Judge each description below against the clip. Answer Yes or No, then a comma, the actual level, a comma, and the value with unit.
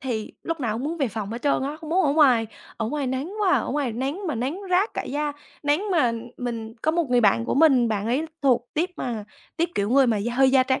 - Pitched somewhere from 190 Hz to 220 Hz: No, very high, 265 Hz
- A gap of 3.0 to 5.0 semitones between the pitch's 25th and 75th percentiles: Yes, average, 4.7 semitones